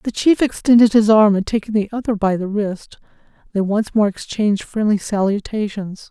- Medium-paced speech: Yes, average, 175 wpm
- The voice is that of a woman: Yes, female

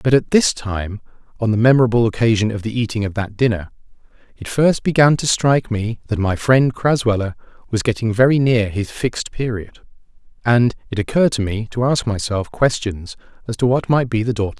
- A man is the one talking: Yes, male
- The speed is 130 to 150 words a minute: No, average, 195 wpm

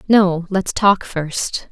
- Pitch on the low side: No, medium, 185 Hz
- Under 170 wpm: Yes, average, 140 wpm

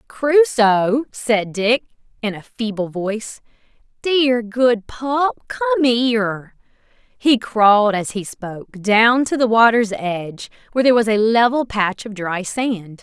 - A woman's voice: Yes, female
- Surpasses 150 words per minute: No, average, 145 wpm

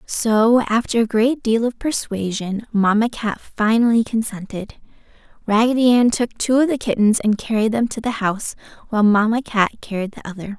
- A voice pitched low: No, high, 225 Hz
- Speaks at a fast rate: No, average, 170 wpm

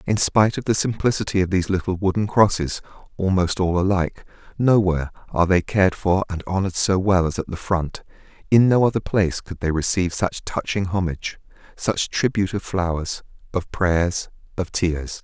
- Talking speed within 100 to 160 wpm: No, average, 175 wpm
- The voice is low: Yes, very low, 95 Hz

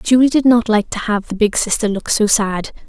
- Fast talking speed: Yes, fast, 250 wpm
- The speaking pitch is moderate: No, high, 220 Hz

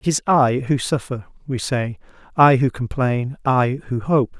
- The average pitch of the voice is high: No, low, 130 Hz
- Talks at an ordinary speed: Yes, average, 180 wpm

